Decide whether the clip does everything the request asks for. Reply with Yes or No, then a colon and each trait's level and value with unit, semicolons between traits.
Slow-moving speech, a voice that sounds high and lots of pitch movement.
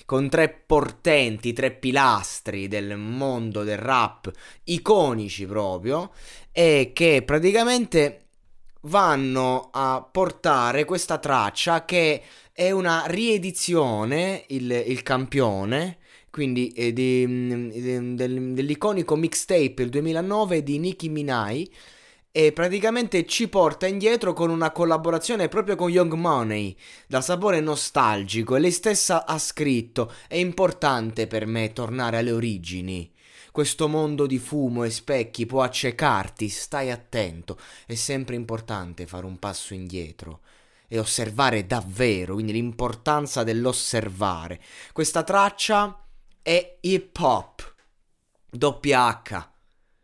No: slow, 110 wpm; low, 135 Hz; wide, 6.3 semitones